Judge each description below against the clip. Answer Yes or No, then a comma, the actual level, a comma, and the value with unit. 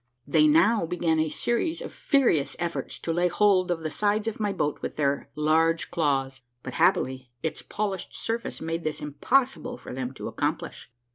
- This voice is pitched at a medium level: Yes, medium, 165 Hz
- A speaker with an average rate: Yes, average, 180 wpm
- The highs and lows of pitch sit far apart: Yes, wide, 5.8 semitones